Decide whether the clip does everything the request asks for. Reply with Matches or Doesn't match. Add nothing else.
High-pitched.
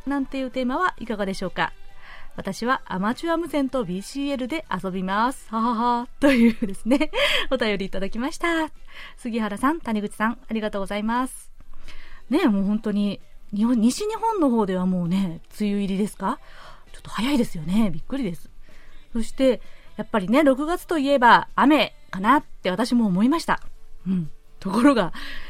Matches